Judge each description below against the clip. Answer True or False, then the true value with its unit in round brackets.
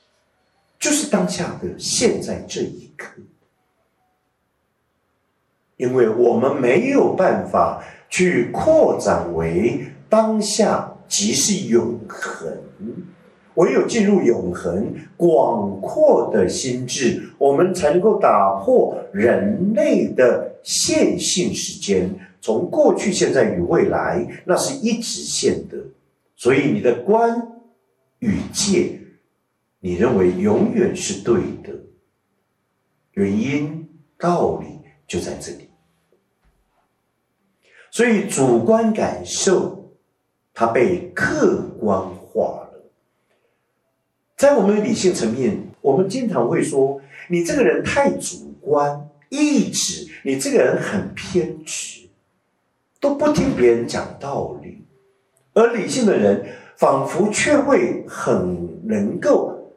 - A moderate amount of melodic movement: False (7.6 semitones)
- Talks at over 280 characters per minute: False (155 characters per minute)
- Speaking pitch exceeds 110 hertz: True (190 Hz)